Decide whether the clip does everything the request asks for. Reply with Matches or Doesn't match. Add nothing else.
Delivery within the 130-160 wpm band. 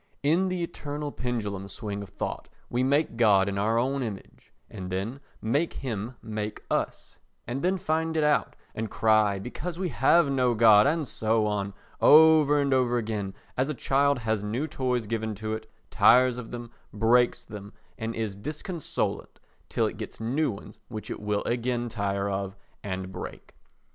Doesn't match